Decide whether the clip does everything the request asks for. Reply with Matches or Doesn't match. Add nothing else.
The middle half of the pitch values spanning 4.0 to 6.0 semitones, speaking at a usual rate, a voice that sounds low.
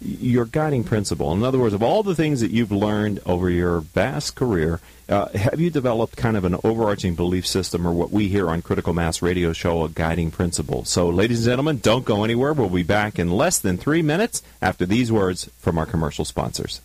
Doesn't match